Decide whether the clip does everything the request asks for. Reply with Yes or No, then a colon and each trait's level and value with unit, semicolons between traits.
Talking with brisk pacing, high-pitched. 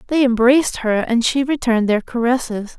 No: average, 175 wpm; high, 245 Hz